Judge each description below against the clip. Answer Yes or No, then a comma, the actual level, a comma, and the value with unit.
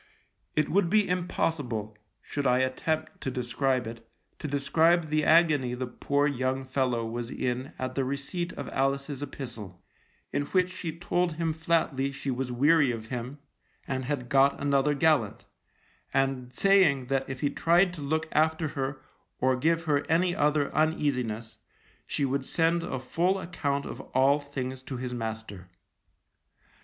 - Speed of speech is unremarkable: Yes, average, 155 wpm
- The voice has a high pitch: No, medium, 140 Hz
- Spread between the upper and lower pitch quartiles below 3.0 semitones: No, average, 3.7 semitones